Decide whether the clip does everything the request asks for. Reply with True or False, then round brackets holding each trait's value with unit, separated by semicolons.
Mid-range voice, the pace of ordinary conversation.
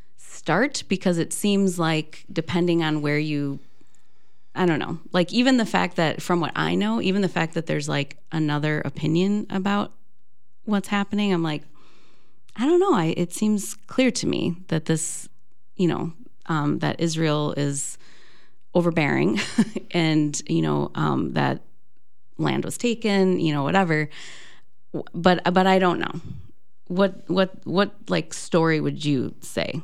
True (170 Hz; 155 wpm)